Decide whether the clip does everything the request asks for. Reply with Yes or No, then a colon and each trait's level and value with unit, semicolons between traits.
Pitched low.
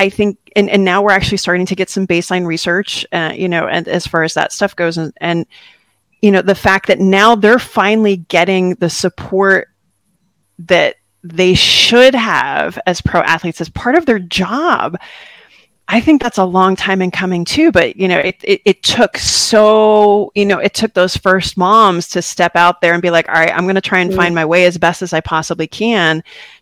No: medium, 185 Hz